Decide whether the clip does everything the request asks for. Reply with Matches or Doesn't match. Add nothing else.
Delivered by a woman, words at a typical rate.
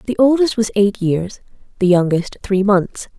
Matches